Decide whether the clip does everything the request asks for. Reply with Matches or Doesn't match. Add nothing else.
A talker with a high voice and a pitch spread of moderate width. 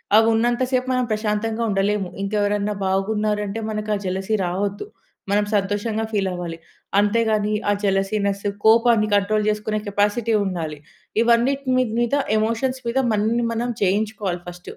Doesn't match